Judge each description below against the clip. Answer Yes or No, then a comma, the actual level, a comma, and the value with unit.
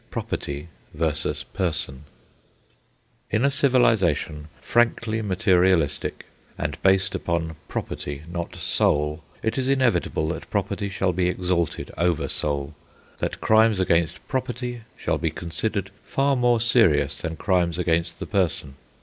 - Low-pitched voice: Yes, very low, 90 Hz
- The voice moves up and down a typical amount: No, wide, 5.8 semitones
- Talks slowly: Yes, slow, 125 wpm